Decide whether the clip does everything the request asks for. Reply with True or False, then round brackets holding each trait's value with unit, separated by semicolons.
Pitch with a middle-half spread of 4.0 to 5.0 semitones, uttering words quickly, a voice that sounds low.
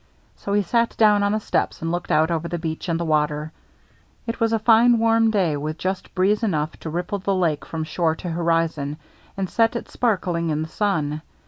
False (4.7 semitones; 220 wpm; 175 Hz)